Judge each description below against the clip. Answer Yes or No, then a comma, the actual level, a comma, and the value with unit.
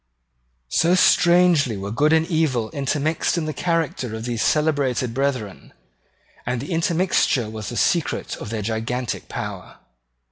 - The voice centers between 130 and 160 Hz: Yes, medium, 140 Hz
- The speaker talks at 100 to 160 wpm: Yes, average, 140 wpm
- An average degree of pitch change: No, wide, 5.9 semitones